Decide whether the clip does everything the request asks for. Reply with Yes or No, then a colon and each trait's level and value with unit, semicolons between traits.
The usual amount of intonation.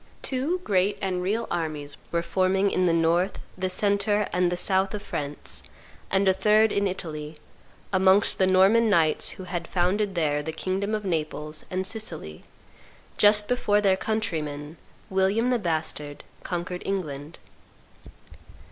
Yes: average, 3.7 semitones